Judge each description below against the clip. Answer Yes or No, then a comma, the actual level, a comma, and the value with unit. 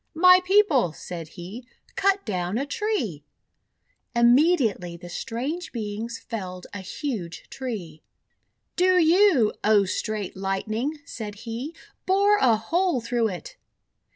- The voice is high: Yes, high, 235 Hz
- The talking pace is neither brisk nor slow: No, slow, 120 wpm